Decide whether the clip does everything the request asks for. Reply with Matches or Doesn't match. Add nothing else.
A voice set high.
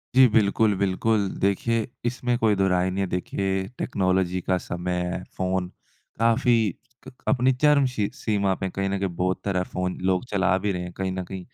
Doesn't match